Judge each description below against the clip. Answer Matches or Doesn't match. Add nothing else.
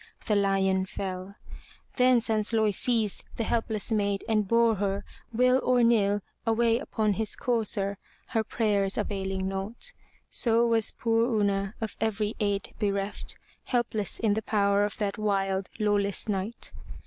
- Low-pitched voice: Doesn't match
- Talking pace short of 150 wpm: Matches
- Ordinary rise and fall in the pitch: Doesn't match